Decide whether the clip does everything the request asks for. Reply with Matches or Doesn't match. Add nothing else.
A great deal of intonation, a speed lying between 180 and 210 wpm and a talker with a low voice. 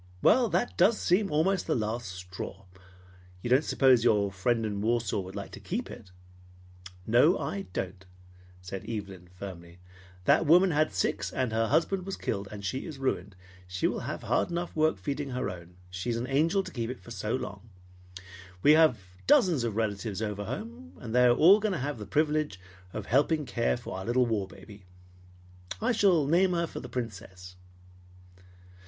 Matches